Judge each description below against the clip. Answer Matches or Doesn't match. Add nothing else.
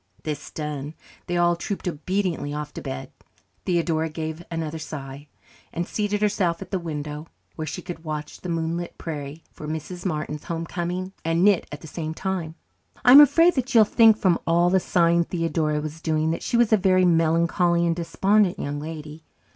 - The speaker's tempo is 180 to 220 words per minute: Matches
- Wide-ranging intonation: Doesn't match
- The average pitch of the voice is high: Doesn't match